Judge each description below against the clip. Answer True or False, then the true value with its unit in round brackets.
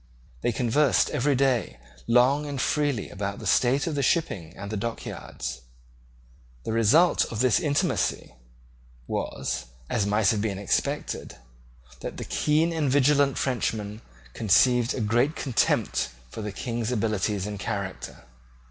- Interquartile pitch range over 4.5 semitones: True (5.1 semitones)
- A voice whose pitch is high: False (120 Hz)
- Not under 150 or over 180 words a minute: False (140 wpm)